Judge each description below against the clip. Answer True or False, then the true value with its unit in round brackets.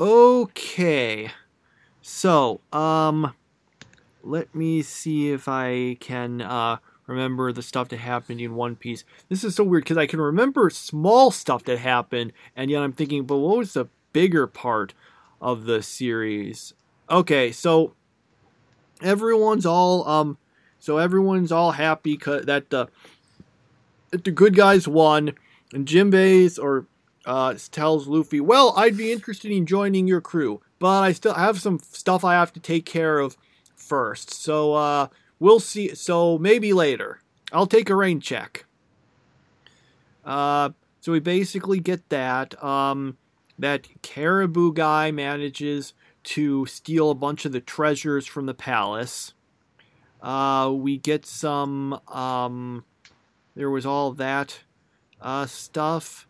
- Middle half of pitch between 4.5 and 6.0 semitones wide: True (5.1 semitones)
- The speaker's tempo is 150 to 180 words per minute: False (140 wpm)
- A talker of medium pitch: True (150 Hz)